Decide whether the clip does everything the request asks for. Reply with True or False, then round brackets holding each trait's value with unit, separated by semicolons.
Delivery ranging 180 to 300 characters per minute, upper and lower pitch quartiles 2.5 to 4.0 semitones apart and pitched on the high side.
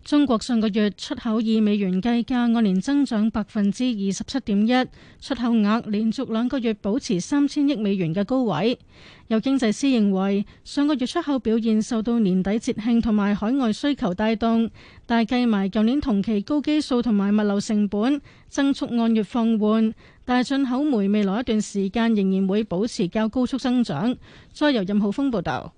True (280 characters per minute; 3.4 semitones; 225 Hz)